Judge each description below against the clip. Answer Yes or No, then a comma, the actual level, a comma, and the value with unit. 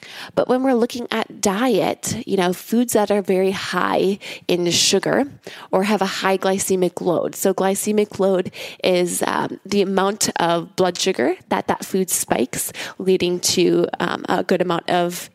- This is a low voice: No, high, 190 Hz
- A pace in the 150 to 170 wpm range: Yes, average, 165 wpm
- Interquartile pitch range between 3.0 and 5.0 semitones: No, narrow, 2.5 semitones